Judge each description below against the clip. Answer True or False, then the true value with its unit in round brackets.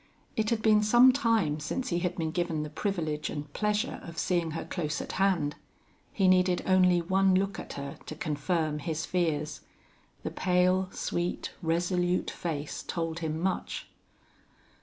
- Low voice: False (175 Hz)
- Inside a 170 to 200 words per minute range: False (160 wpm)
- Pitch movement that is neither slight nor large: True (3.3 semitones)